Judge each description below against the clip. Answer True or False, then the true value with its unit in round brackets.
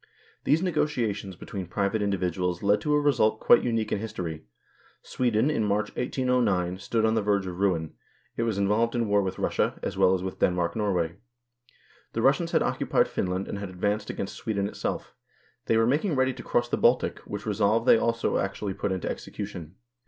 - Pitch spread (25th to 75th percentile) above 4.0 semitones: False (3.5 semitones)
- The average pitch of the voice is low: True (105 Hz)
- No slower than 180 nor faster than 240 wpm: True (190 wpm)